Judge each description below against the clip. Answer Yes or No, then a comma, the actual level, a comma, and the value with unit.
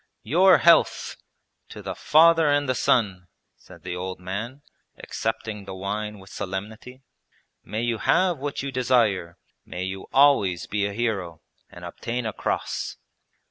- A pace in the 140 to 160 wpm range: Yes, average, 145 wpm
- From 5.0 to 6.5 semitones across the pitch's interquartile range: Yes, wide, 5.6 semitones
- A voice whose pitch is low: Yes, low, 110 Hz